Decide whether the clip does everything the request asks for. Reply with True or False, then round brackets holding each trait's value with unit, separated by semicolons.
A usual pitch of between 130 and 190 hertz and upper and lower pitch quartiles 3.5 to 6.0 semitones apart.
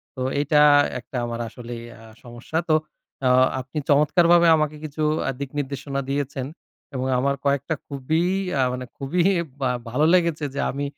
False (140 Hz; 2.9 semitones)